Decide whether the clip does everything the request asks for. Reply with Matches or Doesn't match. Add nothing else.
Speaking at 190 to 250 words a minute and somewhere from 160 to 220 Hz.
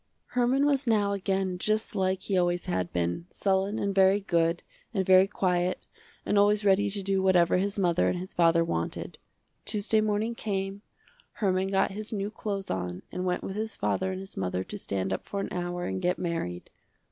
Matches